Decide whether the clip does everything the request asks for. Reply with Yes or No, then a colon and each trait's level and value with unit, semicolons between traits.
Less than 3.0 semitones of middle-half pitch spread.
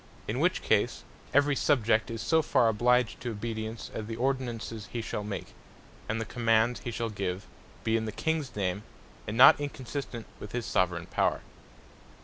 Yes: narrow, 2.5 semitones